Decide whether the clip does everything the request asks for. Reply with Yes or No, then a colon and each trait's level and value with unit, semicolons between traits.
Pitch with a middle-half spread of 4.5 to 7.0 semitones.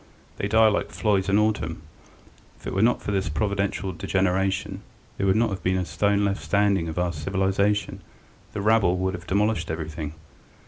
No: narrow, 2.4 semitones